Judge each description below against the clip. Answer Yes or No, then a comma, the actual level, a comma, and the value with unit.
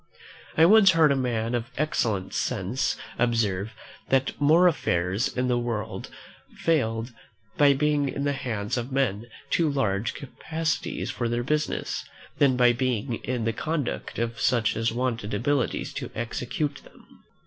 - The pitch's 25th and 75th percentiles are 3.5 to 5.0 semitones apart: Yes, average, 3.9 semitones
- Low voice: Yes, low, 125 Hz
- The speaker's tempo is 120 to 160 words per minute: Yes, average, 150 wpm